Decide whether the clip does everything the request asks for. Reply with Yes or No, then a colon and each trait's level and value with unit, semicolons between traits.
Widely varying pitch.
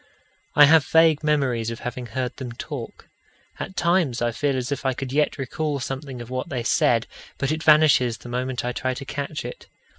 No: average, 3.3 semitones